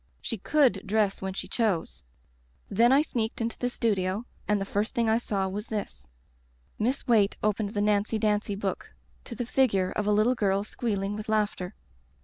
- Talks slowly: No, average, 185 wpm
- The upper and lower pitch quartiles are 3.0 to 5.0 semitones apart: No, narrow, 2.6 semitones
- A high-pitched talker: Yes, high, 210 Hz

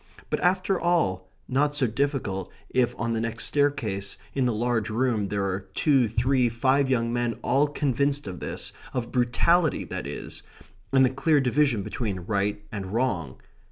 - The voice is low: Yes, low, 120 Hz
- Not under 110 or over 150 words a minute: No, average, 165 wpm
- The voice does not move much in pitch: No, average, 4.9 semitones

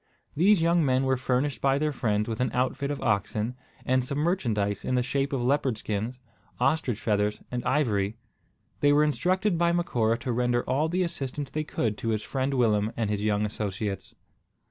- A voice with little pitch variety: No, average, 5.1 semitones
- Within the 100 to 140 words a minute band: No, average, 190 wpm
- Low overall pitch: Yes, low, 125 Hz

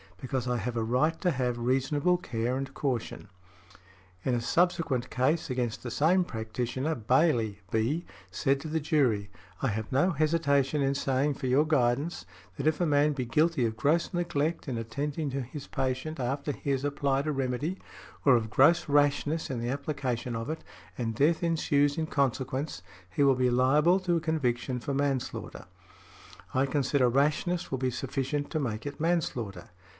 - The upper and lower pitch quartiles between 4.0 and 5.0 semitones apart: No, average, 3.6 semitones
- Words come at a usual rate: Yes, average, 175 wpm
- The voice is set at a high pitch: No, low, 135 Hz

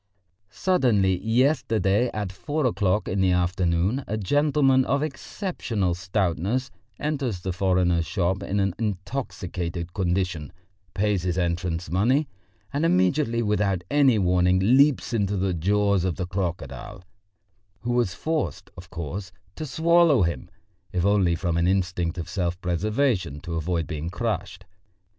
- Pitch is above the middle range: No, very low, 95 Hz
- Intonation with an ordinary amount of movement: Yes, average, 5.0 semitones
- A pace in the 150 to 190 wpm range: No, slow, 135 wpm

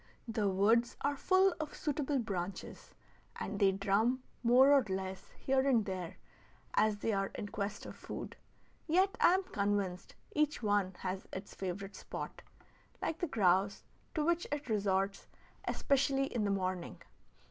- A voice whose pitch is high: Yes, high, 210 Hz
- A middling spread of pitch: No, wide, 6.1 semitones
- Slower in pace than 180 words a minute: Yes, average, 150 wpm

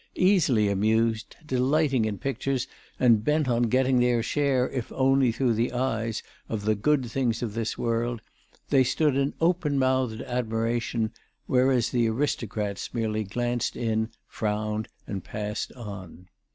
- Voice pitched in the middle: No, low, 120 Hz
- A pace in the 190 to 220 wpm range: No, average, 140 wpm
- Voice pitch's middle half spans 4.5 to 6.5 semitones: No, average, 3.1 semitones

